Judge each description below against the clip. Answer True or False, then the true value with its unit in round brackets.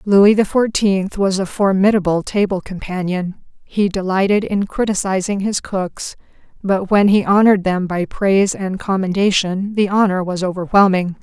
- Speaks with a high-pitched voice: True (195 Hz)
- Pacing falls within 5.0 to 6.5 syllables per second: False (4.7 syllables/s)